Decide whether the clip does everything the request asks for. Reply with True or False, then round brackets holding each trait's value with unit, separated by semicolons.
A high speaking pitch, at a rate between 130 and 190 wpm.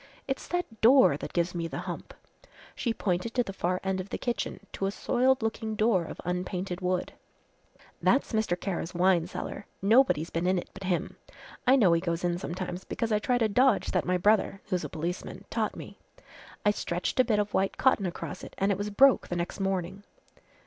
False (195 Hz; 205 wpm)